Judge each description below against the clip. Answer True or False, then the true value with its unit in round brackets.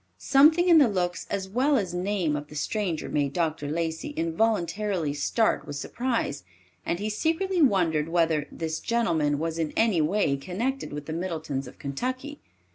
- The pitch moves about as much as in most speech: False (6.5 semitones)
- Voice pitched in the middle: True (175 Hz)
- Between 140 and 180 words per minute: True (165 wpm)